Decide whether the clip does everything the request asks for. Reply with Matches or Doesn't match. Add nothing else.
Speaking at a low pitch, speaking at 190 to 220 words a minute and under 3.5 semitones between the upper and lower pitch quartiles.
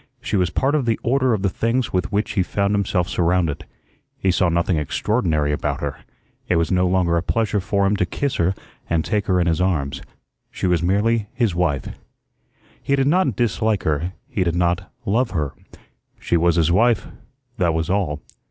Doesn't match